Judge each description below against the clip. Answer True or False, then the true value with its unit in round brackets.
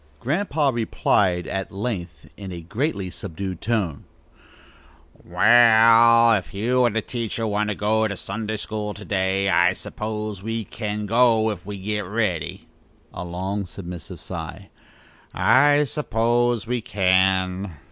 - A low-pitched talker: True (105 Hz)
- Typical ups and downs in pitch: True (3.4 semitones)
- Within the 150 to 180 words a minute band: False (135 wpm)